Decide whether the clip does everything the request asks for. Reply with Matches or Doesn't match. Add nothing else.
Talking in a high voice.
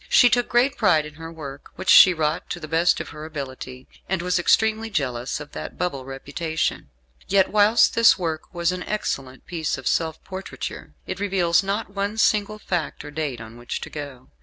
Doesn't match